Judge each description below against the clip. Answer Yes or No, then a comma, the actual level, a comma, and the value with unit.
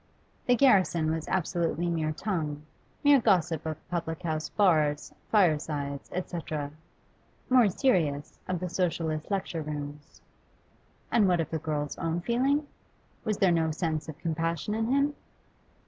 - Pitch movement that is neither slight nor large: Yes, average, 3.8 semitones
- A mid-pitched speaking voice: Yes, medium, 165 Hz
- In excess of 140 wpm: No, slow, 135 wpm